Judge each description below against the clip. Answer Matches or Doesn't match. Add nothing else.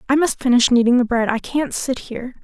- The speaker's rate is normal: Doesn't match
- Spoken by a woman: Matches